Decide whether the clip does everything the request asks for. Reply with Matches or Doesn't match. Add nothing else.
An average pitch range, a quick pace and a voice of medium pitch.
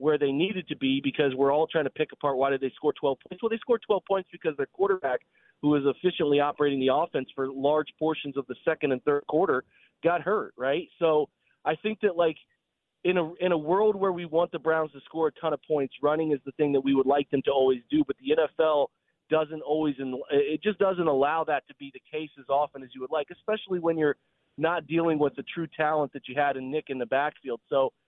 Matches